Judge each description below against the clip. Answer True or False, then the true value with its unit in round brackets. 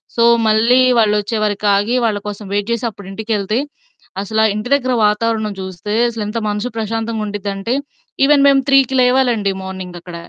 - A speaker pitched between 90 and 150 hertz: False (215 Hz)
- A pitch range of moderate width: False (2.3 semitones)